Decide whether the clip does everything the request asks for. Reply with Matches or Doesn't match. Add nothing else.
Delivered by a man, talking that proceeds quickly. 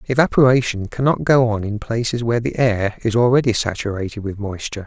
Doesn't match